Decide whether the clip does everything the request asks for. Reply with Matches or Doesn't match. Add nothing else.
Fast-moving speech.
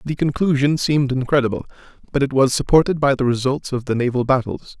Doesn't match